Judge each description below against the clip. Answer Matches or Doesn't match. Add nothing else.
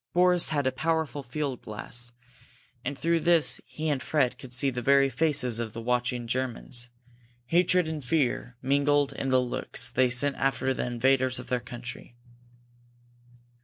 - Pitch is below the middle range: Matches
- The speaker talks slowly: Doesn't match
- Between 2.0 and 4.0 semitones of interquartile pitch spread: Matches